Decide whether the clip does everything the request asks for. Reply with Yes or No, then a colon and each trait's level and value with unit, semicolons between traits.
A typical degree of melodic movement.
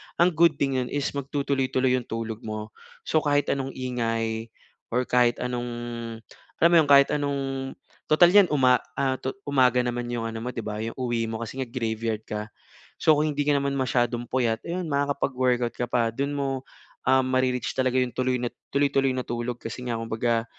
Yes: average, 3.0 semitones